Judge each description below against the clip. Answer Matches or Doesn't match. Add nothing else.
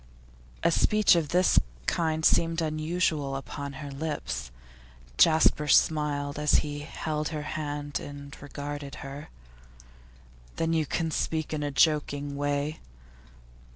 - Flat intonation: Matches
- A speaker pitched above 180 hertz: Doesn't match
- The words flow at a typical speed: Doesn't match